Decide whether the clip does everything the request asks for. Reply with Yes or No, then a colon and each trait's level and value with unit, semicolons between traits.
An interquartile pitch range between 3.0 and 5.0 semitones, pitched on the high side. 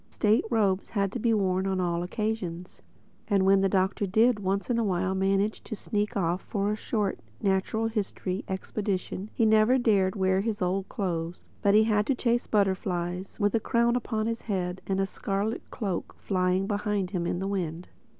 No: narrow, 2.5 semitones; high, 195 Hz